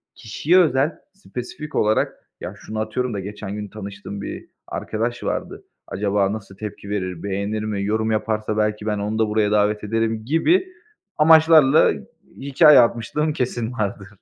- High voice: No, low, 110 Hz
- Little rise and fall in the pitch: No, average, 3.5 semitones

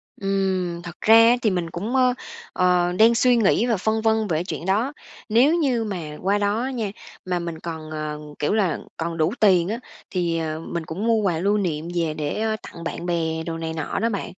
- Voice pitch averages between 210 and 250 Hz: No, medium, 185 Hz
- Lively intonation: No, average, 4.9 semitones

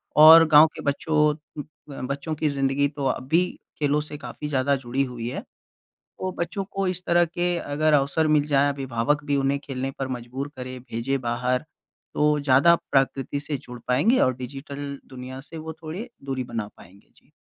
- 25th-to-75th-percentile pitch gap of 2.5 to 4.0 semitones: Yes, average, 3.0 semitones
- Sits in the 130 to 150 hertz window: Yes, medium, 140 Hz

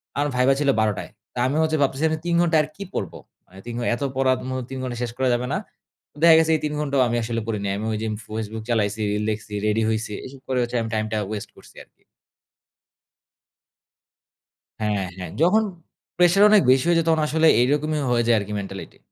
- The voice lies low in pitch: Yes, low, 120 Hz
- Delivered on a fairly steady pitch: No, wide, 5.6 semitones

